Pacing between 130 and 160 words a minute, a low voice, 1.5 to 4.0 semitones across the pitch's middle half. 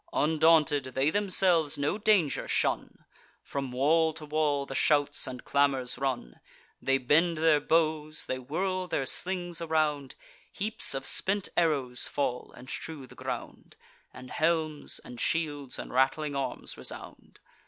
No: average, 140 wpm; medium, 150 Hz; average, 3.3 semitones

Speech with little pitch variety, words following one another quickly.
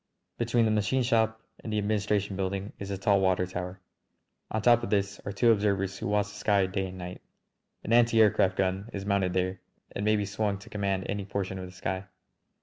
Yes: narrow, 2.1 semitones; fast, 215 wpm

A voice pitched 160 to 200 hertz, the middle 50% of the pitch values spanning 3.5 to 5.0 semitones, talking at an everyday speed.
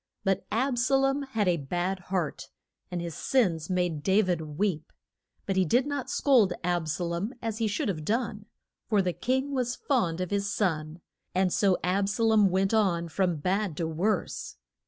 Yes: high, 190 Hz; average, 4.5 semitones; average, 190 wpm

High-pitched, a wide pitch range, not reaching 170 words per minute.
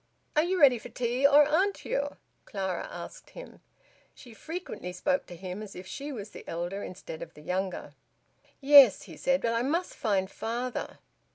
No: high, 235 Hz; wide, 7.1 semitones; average, 180 wpm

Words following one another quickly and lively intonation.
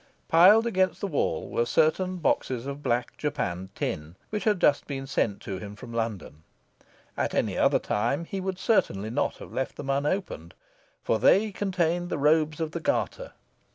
No: average, 175 wpm; wide, 8.0 semitones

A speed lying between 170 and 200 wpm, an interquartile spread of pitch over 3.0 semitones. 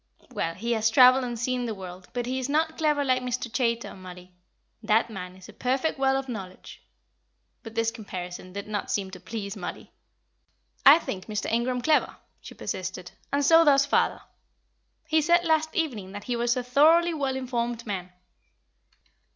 Yes: average, 175 wpm; average, 5.1 semitones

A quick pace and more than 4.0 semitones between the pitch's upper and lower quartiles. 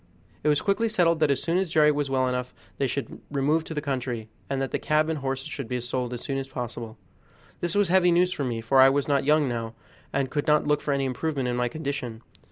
No: fast, 255 wpm; average, 3.5 semitones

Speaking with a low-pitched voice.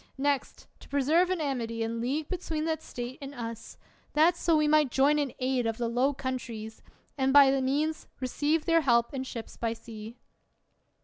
No: very high, 270 Hz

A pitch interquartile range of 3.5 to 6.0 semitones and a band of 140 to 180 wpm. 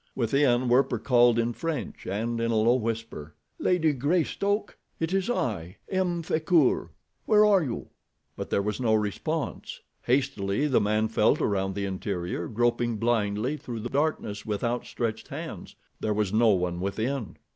Yes: average, 5.2 semitones; average, 155 wpm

